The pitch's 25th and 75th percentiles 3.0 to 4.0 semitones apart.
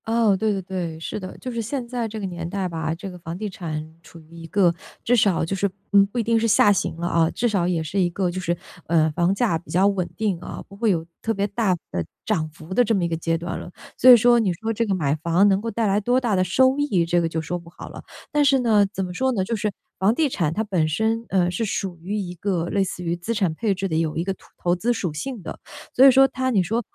No: average, 4.6 semitones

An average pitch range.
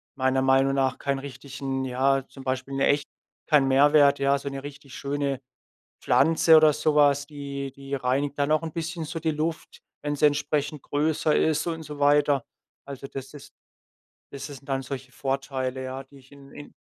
No: narrow, 1.6 semitones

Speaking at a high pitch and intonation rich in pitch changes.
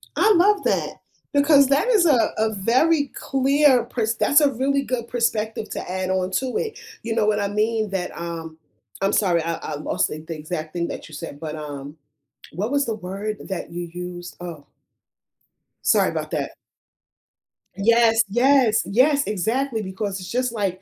Yes: high, 215 Hz; wide, 6.6 semitones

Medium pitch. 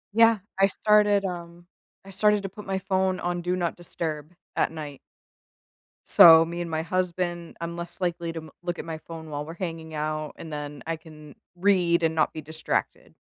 Yes: medium, 170 Hz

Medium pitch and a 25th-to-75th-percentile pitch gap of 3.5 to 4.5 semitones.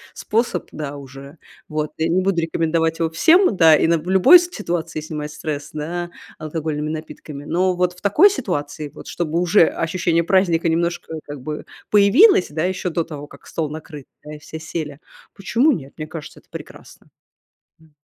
No: medium, 165 Hz; average, 2.9 semitones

